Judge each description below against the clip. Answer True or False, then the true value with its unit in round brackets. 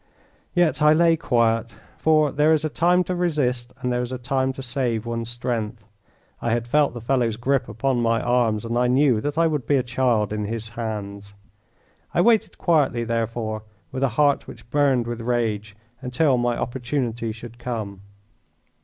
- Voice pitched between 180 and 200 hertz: False (120 Hz)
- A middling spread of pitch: True (3.5 semitones)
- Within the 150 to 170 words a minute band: False (180 wpm)